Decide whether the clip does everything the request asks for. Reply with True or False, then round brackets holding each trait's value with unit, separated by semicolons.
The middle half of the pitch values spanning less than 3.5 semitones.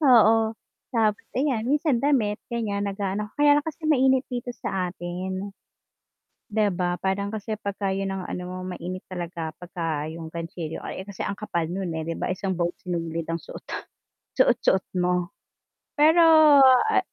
False (4.0 semitones)